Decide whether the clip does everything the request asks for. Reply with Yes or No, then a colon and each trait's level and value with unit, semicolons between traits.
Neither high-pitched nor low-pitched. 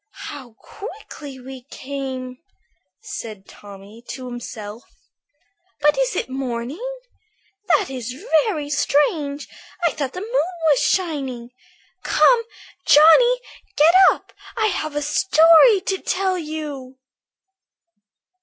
No: very high, 290 Hz